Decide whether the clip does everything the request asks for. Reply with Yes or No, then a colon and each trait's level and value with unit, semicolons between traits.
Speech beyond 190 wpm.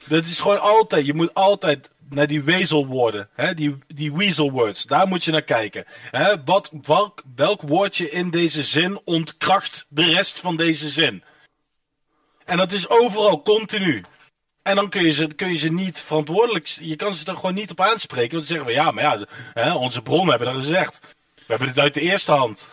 Yes: fast, 200 wpm